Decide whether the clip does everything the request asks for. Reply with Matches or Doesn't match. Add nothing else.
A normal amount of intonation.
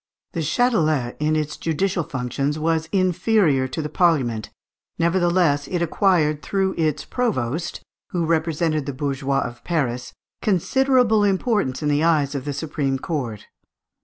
Matches